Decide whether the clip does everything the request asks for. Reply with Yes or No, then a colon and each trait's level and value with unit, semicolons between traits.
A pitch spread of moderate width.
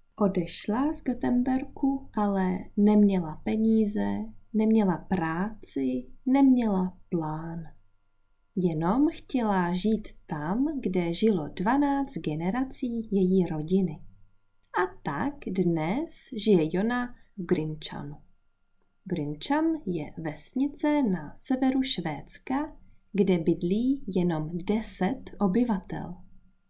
No: wide, 7.4 semitones